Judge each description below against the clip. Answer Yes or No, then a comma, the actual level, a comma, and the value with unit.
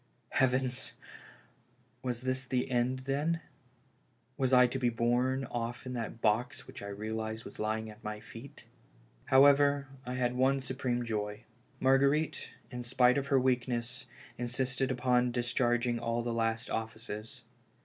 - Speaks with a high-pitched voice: No, low, 125 Hz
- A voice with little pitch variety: Yes, narrow, 2.1 semitones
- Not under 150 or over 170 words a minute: No, average, 140 wpm